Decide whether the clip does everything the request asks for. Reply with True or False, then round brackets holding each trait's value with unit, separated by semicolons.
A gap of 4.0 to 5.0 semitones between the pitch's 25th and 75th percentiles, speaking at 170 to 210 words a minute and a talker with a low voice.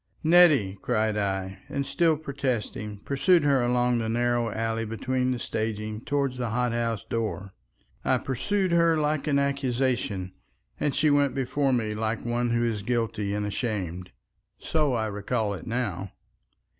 False (4.3 semitones; 155 wpm; 120 Hz)